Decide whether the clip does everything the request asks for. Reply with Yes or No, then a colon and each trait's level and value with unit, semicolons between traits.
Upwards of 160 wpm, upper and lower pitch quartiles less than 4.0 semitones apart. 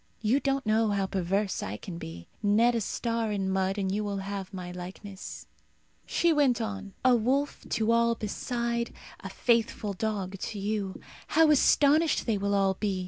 Yes: average, 175 wpm; average, 3.3 semitones